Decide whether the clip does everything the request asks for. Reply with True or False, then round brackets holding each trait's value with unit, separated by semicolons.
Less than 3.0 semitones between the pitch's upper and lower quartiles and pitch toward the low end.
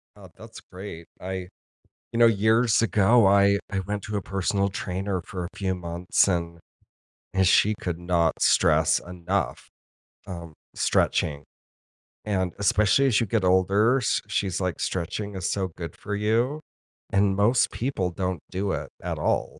True (2.6 semitones; 95 Hz)